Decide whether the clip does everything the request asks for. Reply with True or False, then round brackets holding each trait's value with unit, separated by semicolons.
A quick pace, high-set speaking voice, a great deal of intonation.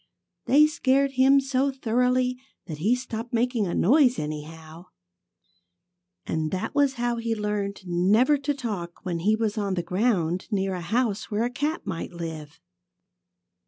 False (155 wpm; 220 Hz; 6.2 semitones)